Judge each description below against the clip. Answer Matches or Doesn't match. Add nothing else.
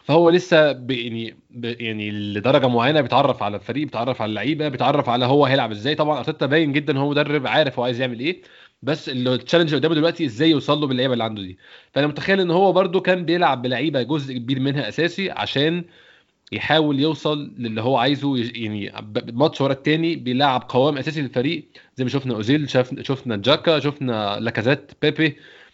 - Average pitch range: Matches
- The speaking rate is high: Matches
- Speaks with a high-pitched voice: Doesn't match